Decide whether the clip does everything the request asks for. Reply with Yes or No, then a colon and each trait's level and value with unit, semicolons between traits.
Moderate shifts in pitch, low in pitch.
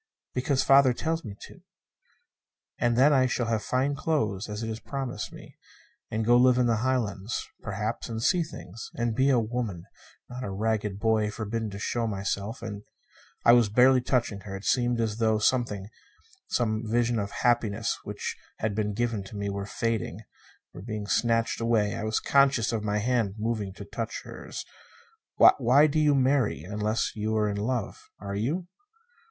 Yes: average, 3.0 semitones; low, 115 Hz